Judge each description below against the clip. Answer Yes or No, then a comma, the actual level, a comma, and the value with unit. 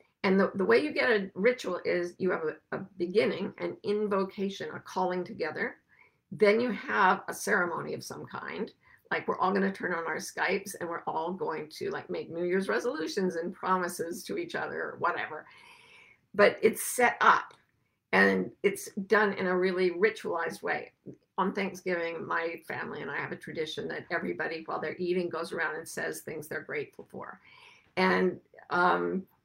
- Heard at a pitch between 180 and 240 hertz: Yes, high, 190 Hz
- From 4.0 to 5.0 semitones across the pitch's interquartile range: No, average, 3.6 semitones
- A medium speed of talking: Yes, average, 180 wpm